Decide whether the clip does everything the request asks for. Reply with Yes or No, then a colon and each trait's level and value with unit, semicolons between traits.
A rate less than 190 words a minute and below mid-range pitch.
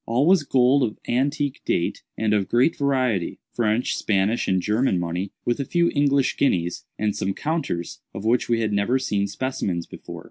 Yes: average, 175 wpm; low, 120 Hz